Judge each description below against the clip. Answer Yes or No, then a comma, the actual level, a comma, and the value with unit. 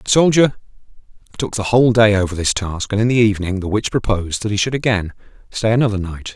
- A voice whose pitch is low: Yes, low, 105 Hz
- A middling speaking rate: No, fast, 215 wpm